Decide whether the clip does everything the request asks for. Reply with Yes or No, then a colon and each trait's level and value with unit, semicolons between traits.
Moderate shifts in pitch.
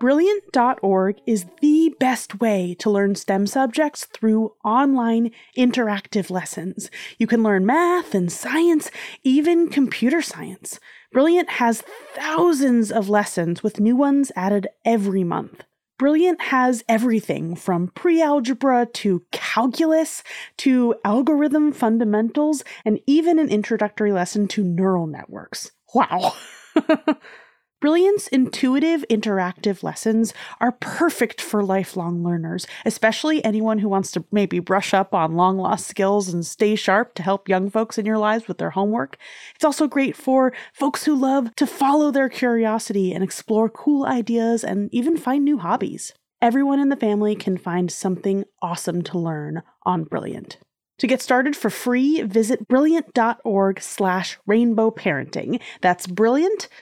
No: wide, 5.8 semitones